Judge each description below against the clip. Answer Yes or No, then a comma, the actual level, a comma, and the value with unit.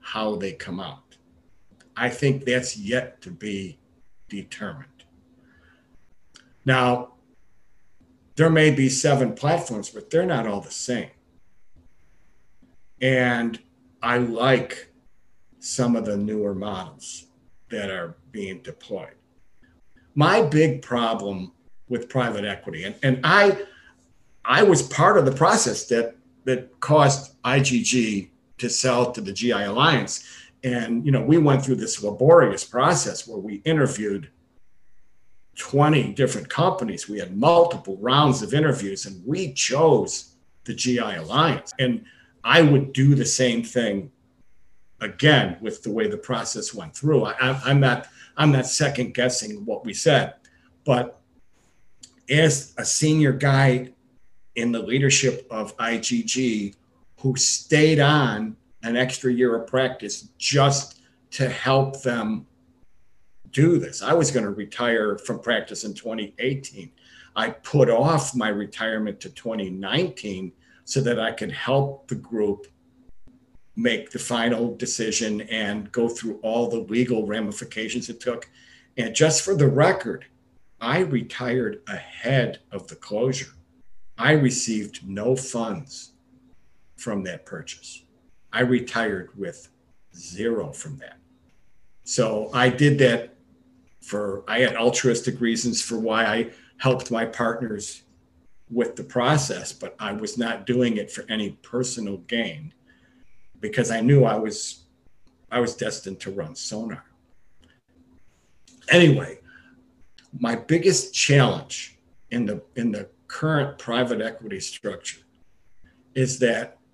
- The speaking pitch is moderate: No, low, 120 Hz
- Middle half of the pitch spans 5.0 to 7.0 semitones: No, average, 3.7 semitones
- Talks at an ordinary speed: No, slow, 125 wpm